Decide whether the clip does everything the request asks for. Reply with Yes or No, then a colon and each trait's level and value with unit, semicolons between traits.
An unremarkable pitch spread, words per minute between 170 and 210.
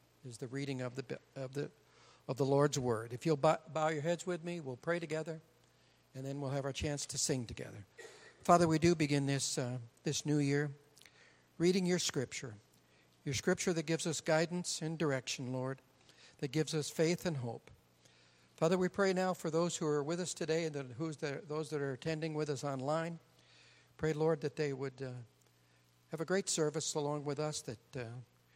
Yes: average, 3.7 semitones; average, 200 wpm